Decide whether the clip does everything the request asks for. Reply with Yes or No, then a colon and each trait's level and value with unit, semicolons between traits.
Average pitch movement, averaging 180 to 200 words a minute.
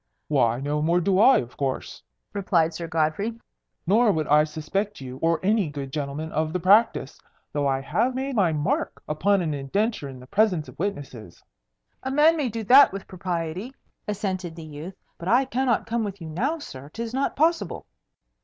No: wide, 6.6 semitones; average, 185 wpm